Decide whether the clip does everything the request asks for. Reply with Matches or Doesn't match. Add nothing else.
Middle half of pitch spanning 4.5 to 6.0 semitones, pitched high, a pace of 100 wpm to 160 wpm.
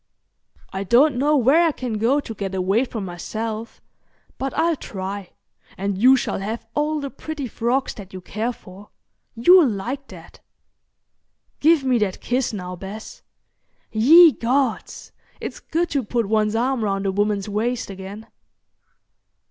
Matches